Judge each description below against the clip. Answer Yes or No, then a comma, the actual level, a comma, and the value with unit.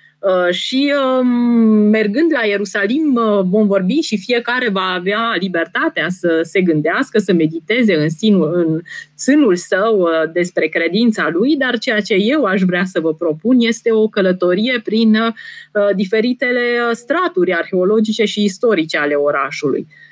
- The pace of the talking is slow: No, average, 130 wpm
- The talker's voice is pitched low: No, high, 210 Hz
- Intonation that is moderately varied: Yes, average, 5.0 semitones